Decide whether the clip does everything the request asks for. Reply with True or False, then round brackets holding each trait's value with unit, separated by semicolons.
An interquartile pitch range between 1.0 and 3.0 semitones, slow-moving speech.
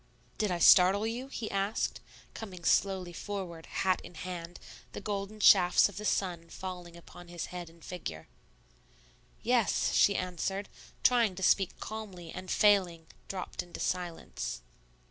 False (2.6 semitones; 145 wpm)